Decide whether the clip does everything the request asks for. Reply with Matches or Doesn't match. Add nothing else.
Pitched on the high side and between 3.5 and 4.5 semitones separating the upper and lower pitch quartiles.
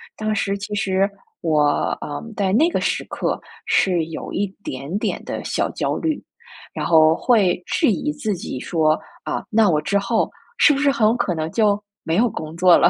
Doesn't match